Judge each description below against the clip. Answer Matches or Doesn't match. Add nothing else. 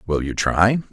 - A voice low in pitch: Matches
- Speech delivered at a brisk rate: Doesn't match